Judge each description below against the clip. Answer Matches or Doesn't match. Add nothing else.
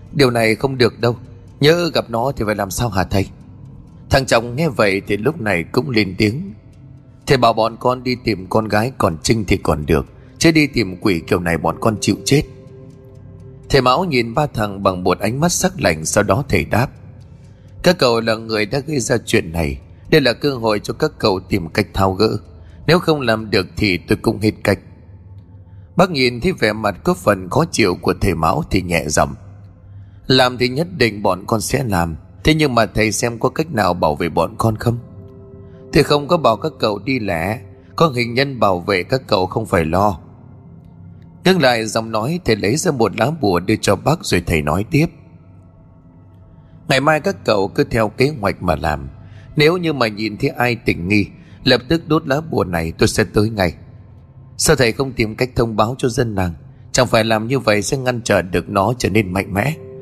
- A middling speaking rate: Matches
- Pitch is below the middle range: Matches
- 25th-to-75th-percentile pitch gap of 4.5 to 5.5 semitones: Matches